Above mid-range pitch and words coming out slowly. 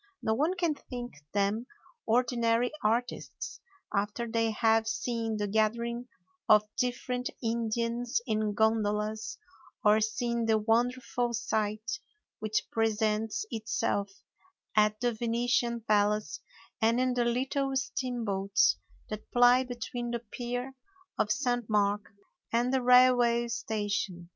Yes: high, 230 Hz; slow, 115 wpm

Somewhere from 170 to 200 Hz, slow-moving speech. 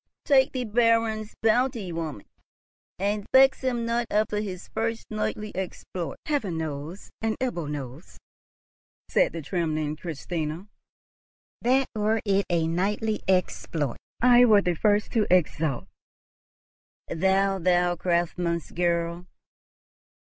Yes: high, 190 Hz; slow, 115 wpm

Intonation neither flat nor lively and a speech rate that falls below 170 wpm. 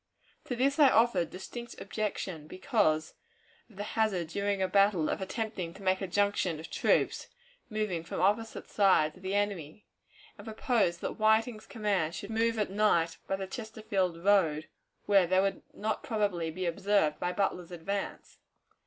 Yes: average, 3.4 semitones; average, 160 wpm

